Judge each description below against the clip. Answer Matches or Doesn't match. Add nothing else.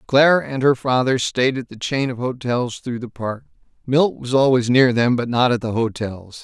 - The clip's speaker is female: Doesn't match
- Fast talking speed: Matches